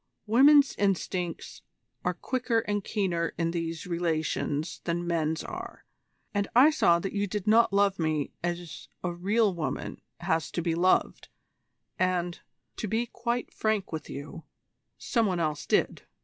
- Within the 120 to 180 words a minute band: Yes, average, 150 wpm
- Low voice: No, medium, 180 Hz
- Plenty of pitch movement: No, average, 4.1 semitones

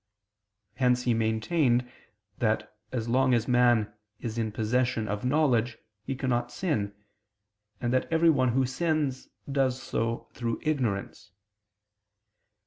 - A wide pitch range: No, narrow, 2.6 semitones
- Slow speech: Yes, slow, 125 wpm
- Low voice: Yes, low, 125 Hz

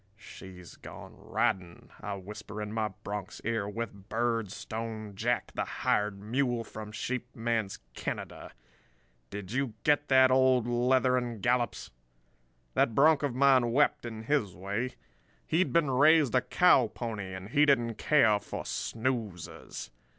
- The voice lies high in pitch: No, low, 115 Hz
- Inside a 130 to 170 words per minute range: Yes, average, 140 wpm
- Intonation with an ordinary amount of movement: Yes, average, 3.8 semitones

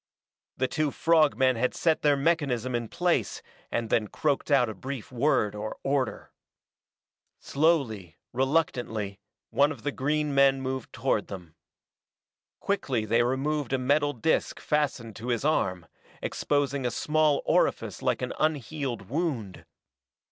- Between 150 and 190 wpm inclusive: No, average, 140 wpm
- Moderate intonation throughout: Yes, average, 4.4 semitones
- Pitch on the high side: No, low, 135 Hz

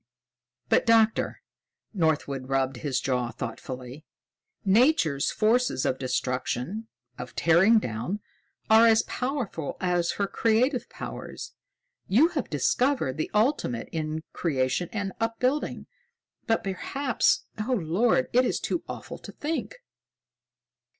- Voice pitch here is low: No, high, 190 Hz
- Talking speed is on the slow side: Yes, slow, 115 wpm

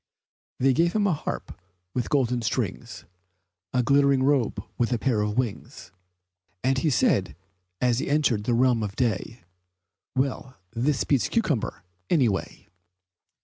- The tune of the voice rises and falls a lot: No, average, 3.4 semitones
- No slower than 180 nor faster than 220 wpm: No, average, 145 wpm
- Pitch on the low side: Yes, low, 125 Hz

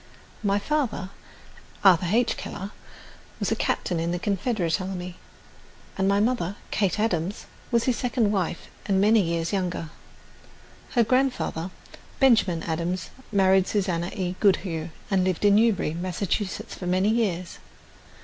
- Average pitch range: Yes, average, 3.3 semitones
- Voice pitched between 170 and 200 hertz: Yes, high, 190 Hz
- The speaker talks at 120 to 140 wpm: Yes, slow, 135 wpm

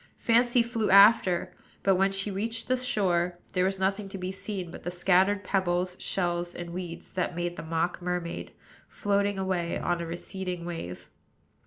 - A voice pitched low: No, medium, 185 Hz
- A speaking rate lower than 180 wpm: Yes, average, 170 wpm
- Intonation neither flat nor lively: No, narrow, 2.3 semitones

